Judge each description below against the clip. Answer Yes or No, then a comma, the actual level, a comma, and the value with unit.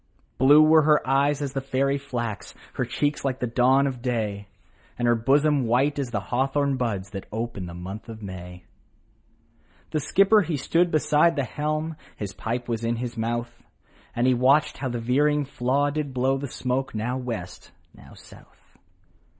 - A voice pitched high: No, low, 130 Hz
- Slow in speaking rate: No, average, 180 wpm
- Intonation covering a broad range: No, average, 3.6 semitones